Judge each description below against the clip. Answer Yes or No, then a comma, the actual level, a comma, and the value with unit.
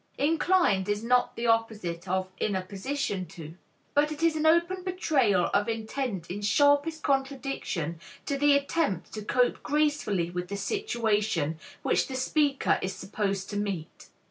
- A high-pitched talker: Yes, high, 225 Hz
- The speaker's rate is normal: Yes, average, 155 wpm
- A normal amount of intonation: No, wide, 7.2 semitones